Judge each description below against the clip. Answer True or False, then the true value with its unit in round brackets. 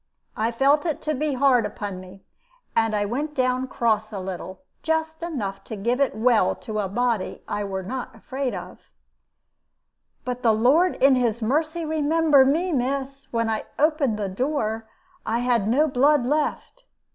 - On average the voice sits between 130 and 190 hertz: False (250 Hz)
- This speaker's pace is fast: False (170 wpm)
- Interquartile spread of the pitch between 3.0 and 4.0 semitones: False (5.1 semitones)